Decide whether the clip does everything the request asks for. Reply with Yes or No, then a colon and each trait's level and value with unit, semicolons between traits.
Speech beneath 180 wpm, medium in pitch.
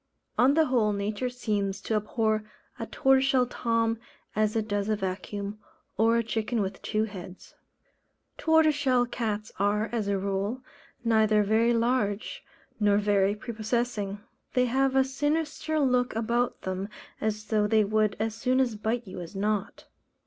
No: average, 150 wpm; high, 220 Hz